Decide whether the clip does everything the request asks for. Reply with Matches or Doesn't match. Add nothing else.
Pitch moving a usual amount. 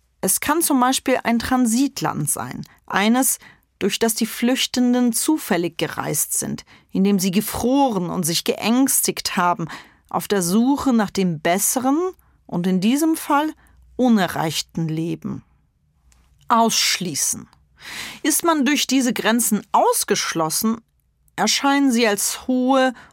Doesn't match